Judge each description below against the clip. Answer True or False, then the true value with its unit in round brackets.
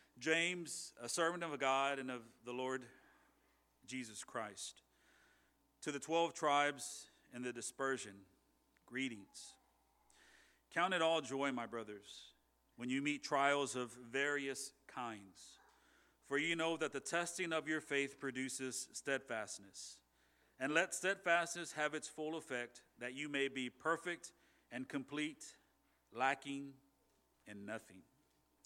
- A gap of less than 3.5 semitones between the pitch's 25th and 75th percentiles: False (3.9 semitones)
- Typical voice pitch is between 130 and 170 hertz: True (135 Hz)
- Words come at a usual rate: False (125 wpm)